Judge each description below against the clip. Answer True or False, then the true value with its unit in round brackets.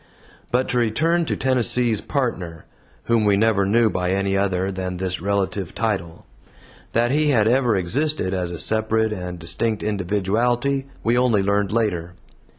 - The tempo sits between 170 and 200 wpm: False (155 wpm)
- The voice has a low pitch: True (105 Hz)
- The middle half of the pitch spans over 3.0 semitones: True (4.2 semitones)